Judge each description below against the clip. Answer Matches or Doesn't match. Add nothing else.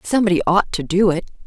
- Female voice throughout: Matches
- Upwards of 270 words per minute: Doesn't match